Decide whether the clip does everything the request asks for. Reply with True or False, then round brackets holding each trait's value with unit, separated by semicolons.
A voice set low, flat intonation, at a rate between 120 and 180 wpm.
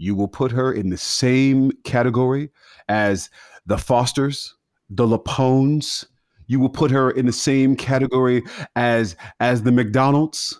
True (130 Hz; 2.2 semitones; 140 wpm)